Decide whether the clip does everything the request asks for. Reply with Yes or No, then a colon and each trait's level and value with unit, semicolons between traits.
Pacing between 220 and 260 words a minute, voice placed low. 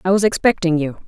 No: fast, 225 wpm; medium, 180 Hz